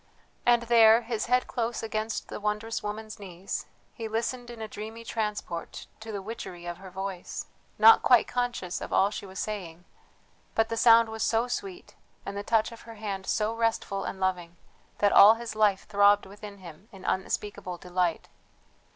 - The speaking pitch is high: Yes, high, 215 Hz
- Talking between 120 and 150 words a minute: No, average, 175 wpm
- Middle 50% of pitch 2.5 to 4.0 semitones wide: Yes, average, 2.9 semitones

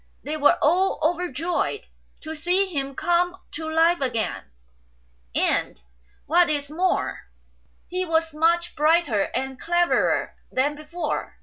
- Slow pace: Yes, slow, 120 wpm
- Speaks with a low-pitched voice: No, very high, 325 Hz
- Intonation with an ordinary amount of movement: Yes, average, 3.0 semitones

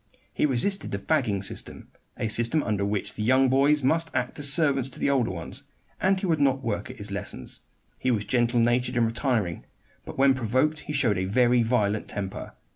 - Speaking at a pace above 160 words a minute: Yes, average, 200 wpm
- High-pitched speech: No, low, 125 Hz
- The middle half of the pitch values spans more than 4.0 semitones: Yes, average, 4.6 semitones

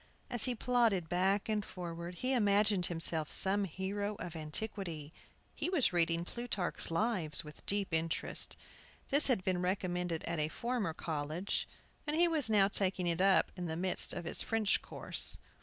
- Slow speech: No, average, 165 wpm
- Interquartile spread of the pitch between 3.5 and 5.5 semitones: Yes, average, 4.0 semitones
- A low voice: No, high, 190 Hz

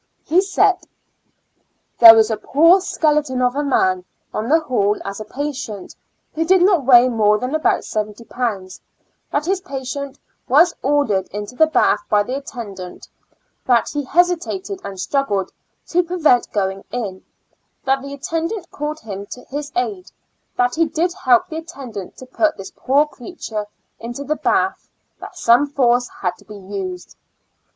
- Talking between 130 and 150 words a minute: No, average, 160 wpm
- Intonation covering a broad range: Yes, wide, 6.8 semitones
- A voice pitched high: Yes, very high, 260 Hz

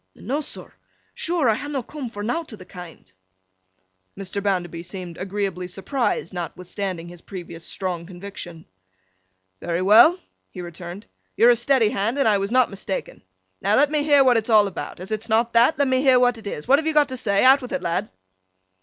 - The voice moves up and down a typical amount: No, wide, 5.9 semitones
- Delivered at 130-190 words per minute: No, average, 200 wpm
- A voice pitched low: No, high, 210 Hz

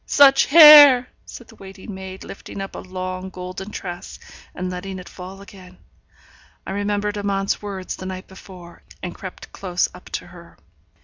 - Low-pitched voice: No, high, 190 Hz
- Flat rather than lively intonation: Yes, narrow, 1.8 semitones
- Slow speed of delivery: No, average, 165 wpm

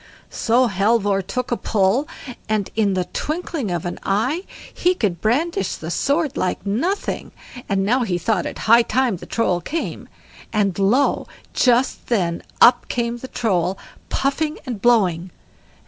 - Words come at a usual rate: Yes, average, 150 wpm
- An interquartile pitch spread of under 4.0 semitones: No, average, 5.1 semitones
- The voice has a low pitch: No, high, 230 Hz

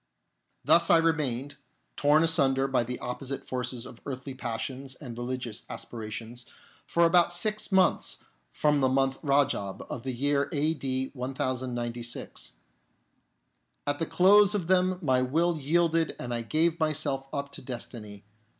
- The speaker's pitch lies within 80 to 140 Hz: Yes, low, 135 Hz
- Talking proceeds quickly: No, average, 140 wpm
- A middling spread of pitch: Yes, average, 4.4 semitones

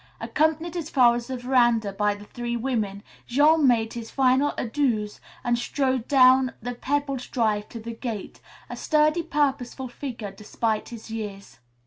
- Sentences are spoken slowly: No, average, 155 wpm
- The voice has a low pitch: No, high, 245 Hz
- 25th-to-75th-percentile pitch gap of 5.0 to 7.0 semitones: No, average, 3.5 semitones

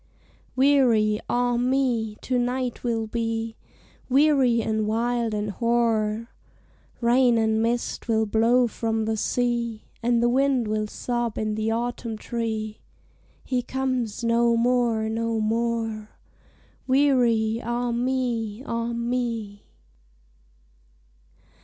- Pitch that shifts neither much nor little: No, narrow, 1.7 semitones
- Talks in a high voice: Yes, high, 235 Hz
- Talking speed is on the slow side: Yes, slow, 110 wpm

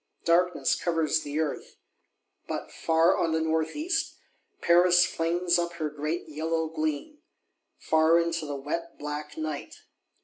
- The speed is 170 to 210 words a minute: No, slow, 135 wpm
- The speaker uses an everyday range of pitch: No, narrow, 1.8 semitones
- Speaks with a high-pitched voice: No, medium, 160 Hz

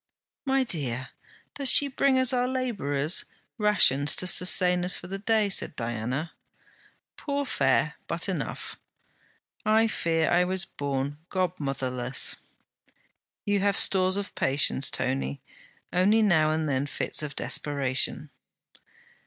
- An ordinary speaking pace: No, slow, 125 wpm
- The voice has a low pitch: No, medium, 180 Hz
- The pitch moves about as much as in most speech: No, wide, 6.9 semitones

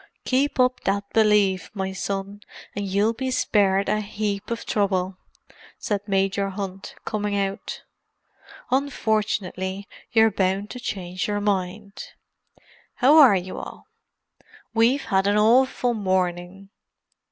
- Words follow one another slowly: Yes, slow, 120 wpm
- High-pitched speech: Yes, high, 200 Hz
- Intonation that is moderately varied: No, narrow, 2.3 semitones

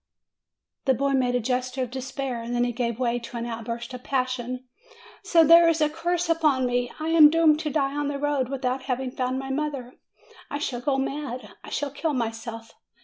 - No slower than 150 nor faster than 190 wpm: No, fast, 205 wpm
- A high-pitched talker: Yes, very high, 260 Hz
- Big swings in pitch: No, average, 3.1 semitones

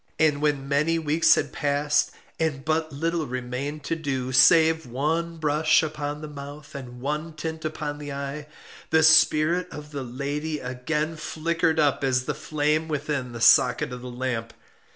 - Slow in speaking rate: No, average, 165 wpm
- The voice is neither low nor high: Yes, medium, 150 Hz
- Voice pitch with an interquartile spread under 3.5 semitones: Yes, narrow, 2.5 semitones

